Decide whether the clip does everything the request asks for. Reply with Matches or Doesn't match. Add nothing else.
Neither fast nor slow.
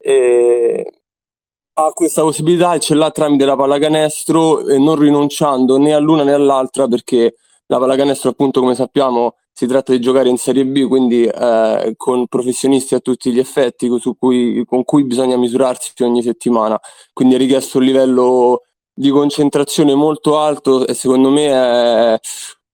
Matches